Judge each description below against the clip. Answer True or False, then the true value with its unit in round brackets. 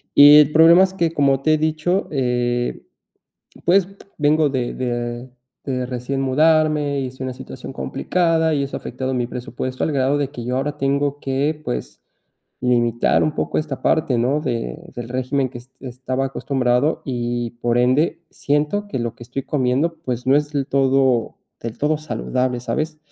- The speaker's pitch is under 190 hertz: True (135 Hz)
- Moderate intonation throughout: True (3.4 semitones)